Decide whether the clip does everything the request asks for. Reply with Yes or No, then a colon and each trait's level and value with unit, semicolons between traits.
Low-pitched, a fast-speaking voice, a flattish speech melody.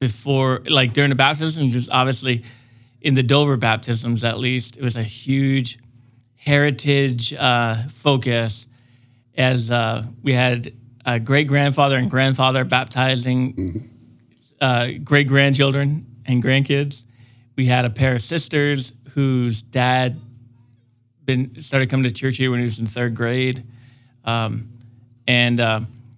No: low, 125 Hz; slow, 135 wpm; narrow, 2.1 semitones